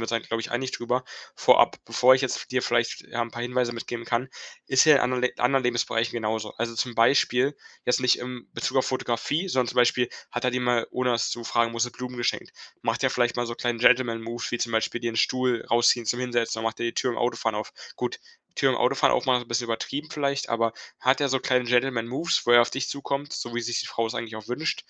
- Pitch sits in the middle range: No, low, 120 Hz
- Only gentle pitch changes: Yes, narrow, 1.5 semitones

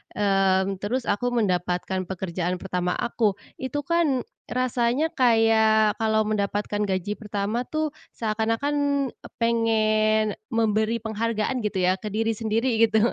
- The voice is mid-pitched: No, high, 220 Hz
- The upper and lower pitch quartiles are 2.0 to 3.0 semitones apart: Yes, narrow, 2.5 semitones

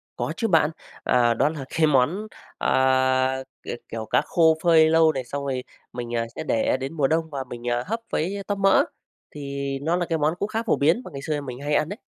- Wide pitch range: No, average, 3.8 semitones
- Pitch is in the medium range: Yes, medium, 145 Hz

